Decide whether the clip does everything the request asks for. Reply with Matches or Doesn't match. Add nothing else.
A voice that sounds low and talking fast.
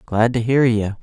Matches